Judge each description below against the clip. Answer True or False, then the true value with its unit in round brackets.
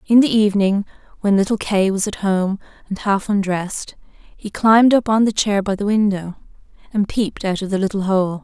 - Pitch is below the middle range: False (200 Hz)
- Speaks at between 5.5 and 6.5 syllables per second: False (5.3 syllables/s)